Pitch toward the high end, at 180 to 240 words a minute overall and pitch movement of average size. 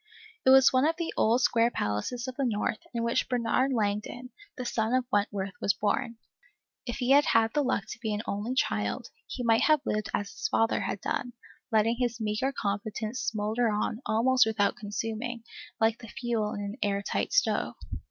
Yes: high, 230 Hz; average, 190 wpm; average, 3.0 semitones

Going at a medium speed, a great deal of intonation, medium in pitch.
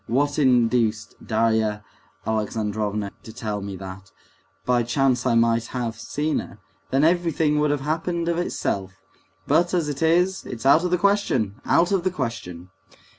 No: average, 160 wpm; wide, 6.5 semitones; low, 125 Hz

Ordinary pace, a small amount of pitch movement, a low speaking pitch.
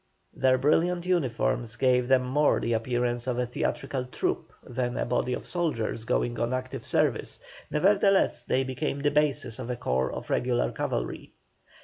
No: average, 160 wpm; average, 3.2 semitones; low, 130 Hz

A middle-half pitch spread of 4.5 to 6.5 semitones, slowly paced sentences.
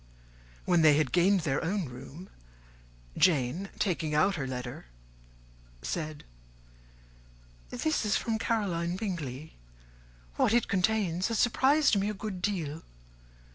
Yes: average, 5.2 semitones; slow, 120 wpm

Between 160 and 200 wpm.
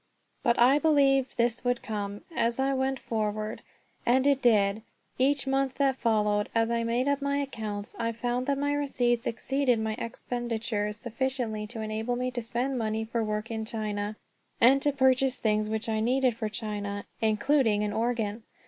Yes: average, 175 wpm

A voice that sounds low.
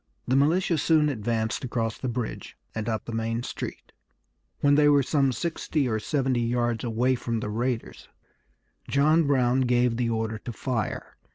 Yes: low, 125 Hz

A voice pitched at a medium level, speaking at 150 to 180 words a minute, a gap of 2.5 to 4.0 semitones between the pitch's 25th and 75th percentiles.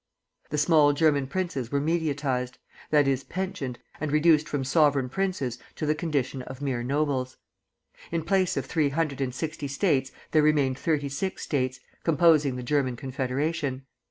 Yes: medium, 145 Hz; average, 155 wpm; average, 2.9 semitones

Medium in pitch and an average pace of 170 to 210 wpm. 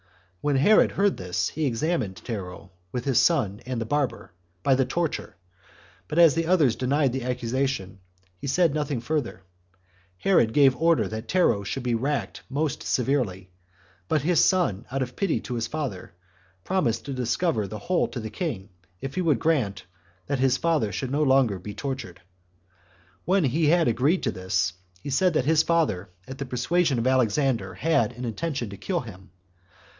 No: low, 130 Hz; average, 180 wpm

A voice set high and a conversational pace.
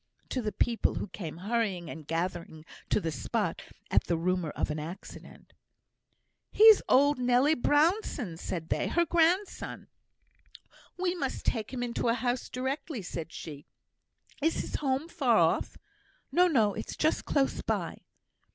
Yes: high, 240 Hz; average, 150 wpm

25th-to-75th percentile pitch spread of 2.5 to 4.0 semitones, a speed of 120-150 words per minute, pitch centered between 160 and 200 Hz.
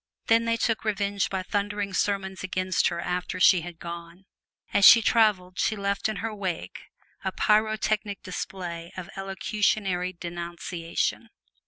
Yes: average, 2.9 semitones; average, 140 wpm; high, 190 Hz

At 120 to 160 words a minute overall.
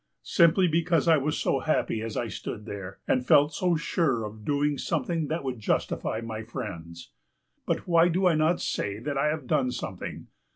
No: average, 190 wpm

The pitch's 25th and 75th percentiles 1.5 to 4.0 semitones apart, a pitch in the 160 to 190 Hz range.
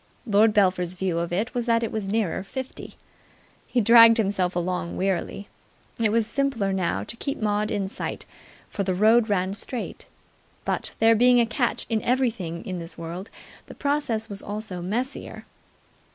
No: average, 3.6 semitones; high, 210 Hz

